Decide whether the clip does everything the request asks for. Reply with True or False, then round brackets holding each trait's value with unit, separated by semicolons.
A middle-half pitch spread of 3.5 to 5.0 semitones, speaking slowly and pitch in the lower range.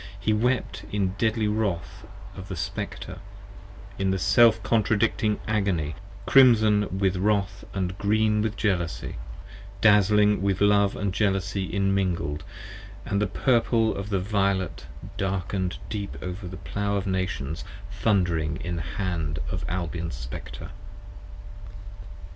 False (2.5 semitones; 125 wpm; 100 Hz)